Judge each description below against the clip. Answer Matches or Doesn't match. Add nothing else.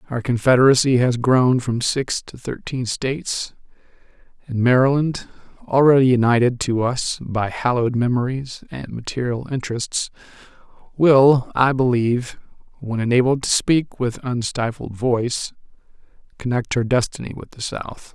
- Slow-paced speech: Matches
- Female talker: Doesn't match